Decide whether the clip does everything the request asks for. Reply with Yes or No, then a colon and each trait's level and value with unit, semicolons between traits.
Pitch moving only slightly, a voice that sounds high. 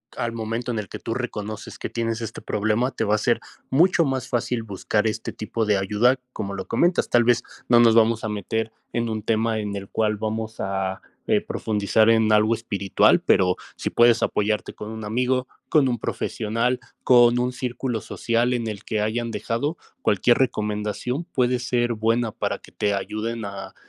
No: narrow, 2.2 semitones; low, 115 Hz